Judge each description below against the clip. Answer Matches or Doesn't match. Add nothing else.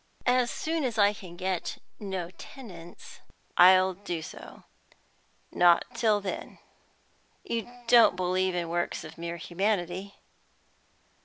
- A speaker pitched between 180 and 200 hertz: Matches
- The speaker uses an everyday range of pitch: Matches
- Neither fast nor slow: Doesn't match